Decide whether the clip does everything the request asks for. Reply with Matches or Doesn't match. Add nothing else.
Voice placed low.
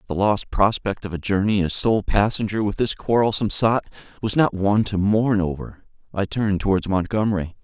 Matches